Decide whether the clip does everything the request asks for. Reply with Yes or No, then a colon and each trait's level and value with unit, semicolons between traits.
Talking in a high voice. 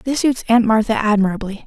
Yes: high, 225 Hz